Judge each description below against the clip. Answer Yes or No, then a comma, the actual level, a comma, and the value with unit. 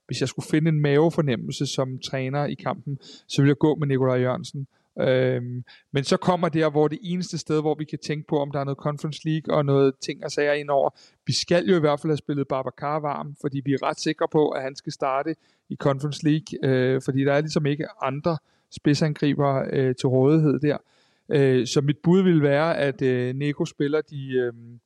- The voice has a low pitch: No, medium, 145 Hz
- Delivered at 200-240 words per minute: Yes, average, 220 wpm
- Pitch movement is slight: Yes, narrow, 2.3 semitones